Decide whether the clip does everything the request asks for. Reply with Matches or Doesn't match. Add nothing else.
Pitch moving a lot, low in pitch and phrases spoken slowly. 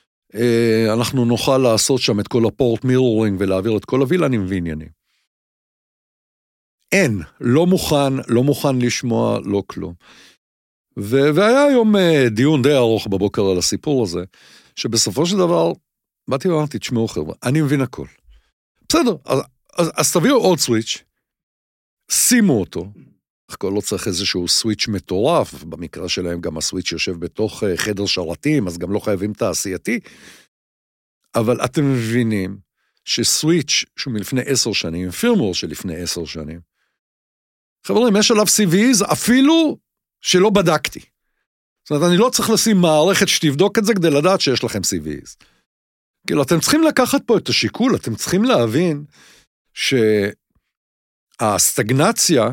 Matches